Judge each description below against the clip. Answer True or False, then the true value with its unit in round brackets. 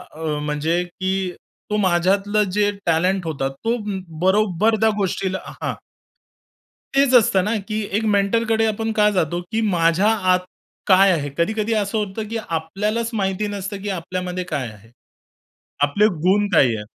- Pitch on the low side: False (195 Hz)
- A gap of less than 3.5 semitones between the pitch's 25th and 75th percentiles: False (3.9 semitones)